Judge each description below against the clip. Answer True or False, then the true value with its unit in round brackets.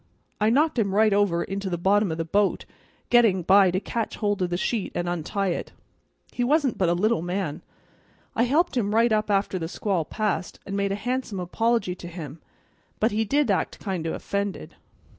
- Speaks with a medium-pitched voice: False (200 Hz)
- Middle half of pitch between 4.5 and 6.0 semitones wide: False (3.8 semitones)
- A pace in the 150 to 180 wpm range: False (200 wpm)